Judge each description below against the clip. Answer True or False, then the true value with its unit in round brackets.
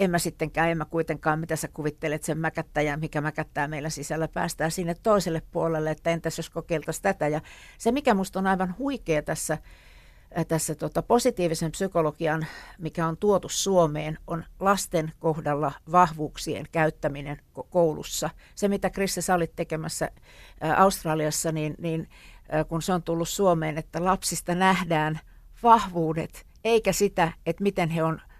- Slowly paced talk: False (150 wpm)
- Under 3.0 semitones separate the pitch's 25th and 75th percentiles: True (2.6 semitones)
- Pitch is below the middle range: False (165 Hz)